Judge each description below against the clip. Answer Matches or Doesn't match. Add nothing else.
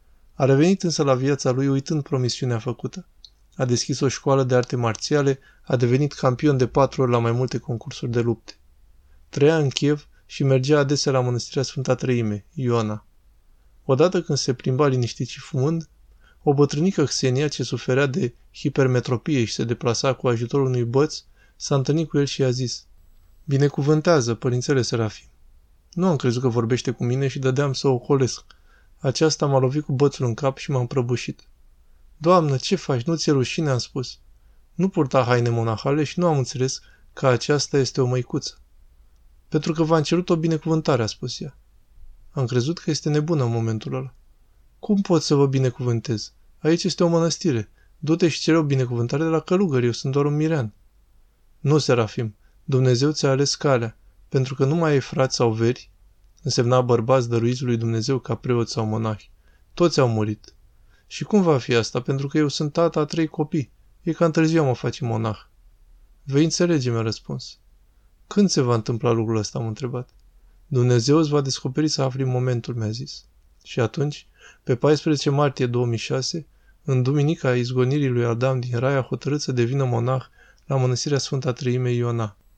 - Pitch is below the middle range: Matches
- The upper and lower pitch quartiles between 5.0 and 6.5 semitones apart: Doesn't match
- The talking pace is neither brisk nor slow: Doesn't match